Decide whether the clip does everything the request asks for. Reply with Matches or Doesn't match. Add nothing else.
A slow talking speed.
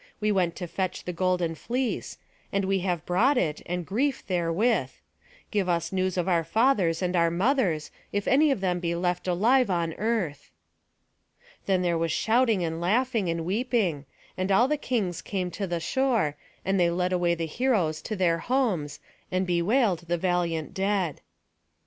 Doesn't match